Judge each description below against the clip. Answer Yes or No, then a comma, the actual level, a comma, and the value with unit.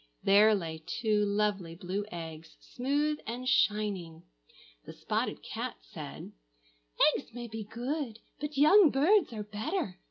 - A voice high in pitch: Yes, high, 215 Hz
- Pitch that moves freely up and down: Yes, wide, 5.7 semitones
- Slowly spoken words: Yes, slow, 130 wpm